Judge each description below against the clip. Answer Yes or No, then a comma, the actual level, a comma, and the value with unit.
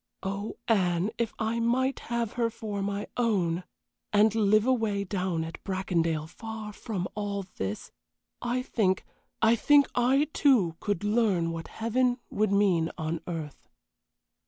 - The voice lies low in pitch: No, high, 205 Hz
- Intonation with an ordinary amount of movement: Yes, average, 4.3 semitones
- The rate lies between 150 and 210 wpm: No, average, 140 wpm